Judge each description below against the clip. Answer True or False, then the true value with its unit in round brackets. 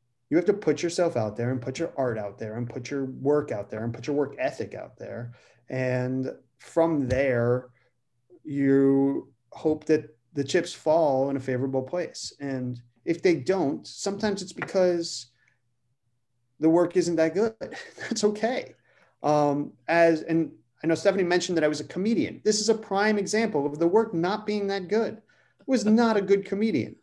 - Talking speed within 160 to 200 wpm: True (185 wpm)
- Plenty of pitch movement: True (6.6 semitones)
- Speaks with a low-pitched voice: False (150 Hz)